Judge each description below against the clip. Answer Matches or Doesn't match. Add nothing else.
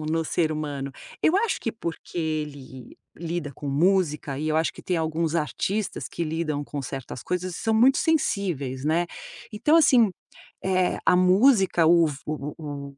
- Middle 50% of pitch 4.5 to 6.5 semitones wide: Doesn't match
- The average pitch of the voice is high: Doesn't match